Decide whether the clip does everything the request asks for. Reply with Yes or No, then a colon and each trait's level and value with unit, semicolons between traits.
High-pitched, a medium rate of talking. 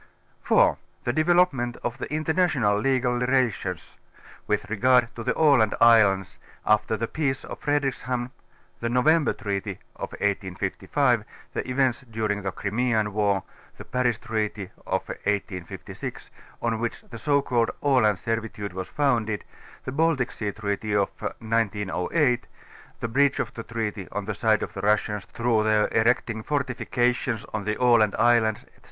No: low, 115 Hz; average, 150 wpm